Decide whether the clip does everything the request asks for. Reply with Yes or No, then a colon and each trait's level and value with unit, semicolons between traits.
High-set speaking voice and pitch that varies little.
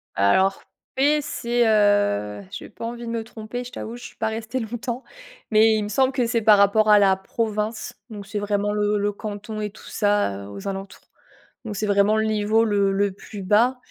Yes: high, 210 Hz; narrow, 2.1 semitones